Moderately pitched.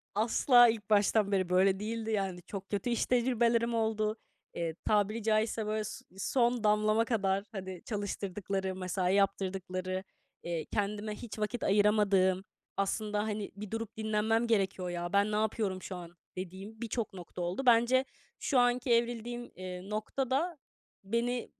No: high, 210 Hz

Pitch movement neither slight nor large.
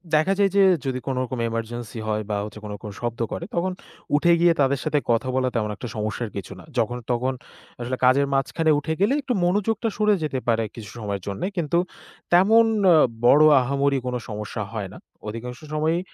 No: wide, 5.9 semitones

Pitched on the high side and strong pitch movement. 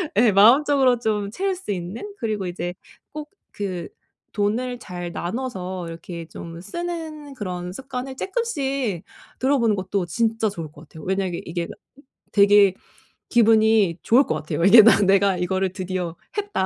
Yes: high, 205 Hz; wide, 6.0 semitones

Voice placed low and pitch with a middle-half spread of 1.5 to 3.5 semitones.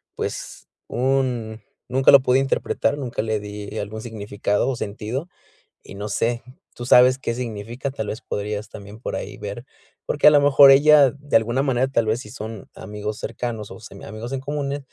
No: low, 120 Hz; average, 4.0 semitones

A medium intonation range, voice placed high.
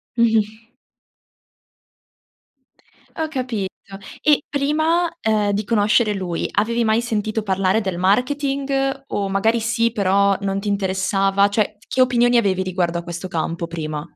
Yes: average, 3.8 semitones; high, 210 Hz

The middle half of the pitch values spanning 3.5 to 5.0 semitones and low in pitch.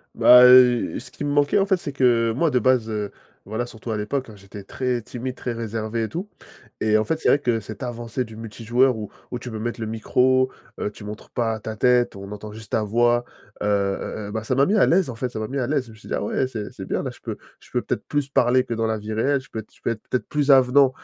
No: average, 2.9 semitones; low, 120 Hz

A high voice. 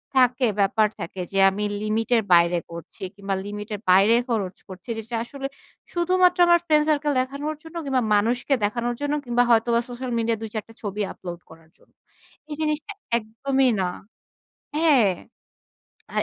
Yes: high, 230 Hz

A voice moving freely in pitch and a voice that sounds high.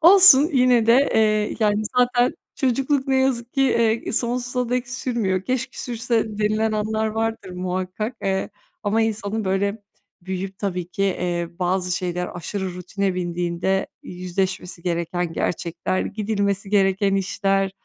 No: average, 4.2 semitones; high, 205 Hz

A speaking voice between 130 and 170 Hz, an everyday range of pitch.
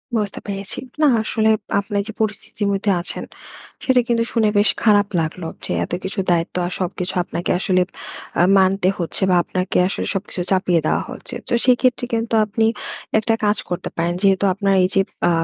No: high, 200 Hz; average, 3.0 semitones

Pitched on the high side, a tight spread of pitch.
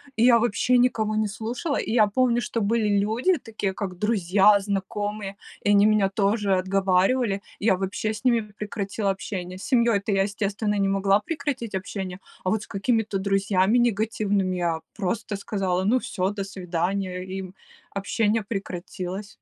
Yes: high, 200 Hz; narrow, 2.3 semitones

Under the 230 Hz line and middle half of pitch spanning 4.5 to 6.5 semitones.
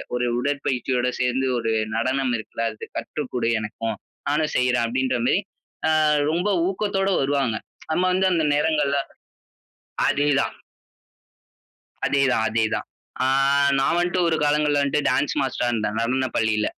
No: low, 135 Hz; average, 3.8 semitones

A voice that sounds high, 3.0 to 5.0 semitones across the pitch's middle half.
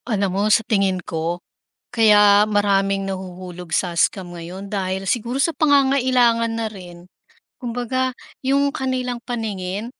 Yes: high, 210 Hz; average, 4.6 semitones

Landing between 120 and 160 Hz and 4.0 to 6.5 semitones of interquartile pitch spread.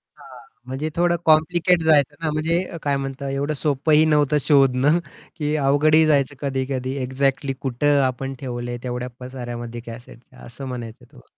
No: medium, 140 Hz; average, 2.9 semitones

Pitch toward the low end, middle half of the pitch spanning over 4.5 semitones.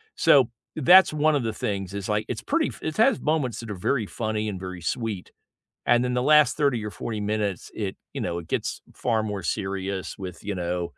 Yes: low, 110 Hz; average, 5.2 semitones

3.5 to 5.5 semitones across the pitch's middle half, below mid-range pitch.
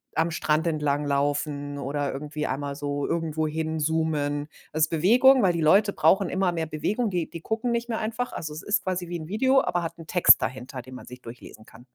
No: average, 4.2 semitones; medium, 160 Hz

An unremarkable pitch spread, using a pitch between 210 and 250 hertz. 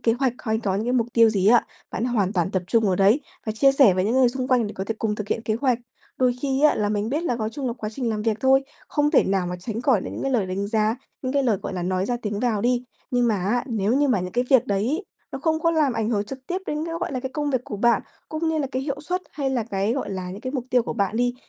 Yes: average, 4.3 semitones; high, 235 Hz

